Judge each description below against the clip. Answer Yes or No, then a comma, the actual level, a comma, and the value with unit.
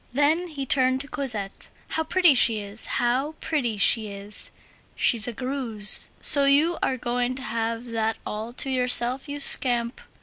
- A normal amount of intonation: Yes, average, 3.6 semitones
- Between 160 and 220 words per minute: Yes, average, 165 wpm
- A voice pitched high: Yes, very high, 250 Hz